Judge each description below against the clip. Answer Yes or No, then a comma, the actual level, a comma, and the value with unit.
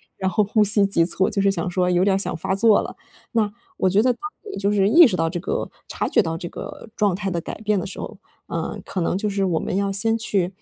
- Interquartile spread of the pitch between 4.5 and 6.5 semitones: No, narrow, 2.5 semitones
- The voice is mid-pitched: No, high, 195 Hz